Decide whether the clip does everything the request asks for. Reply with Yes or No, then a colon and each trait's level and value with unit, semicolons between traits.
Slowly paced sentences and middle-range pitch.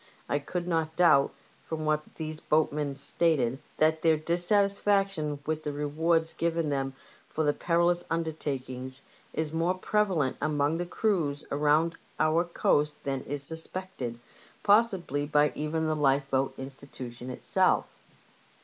Yes: slow, 130 wpm; medium, 155 Hz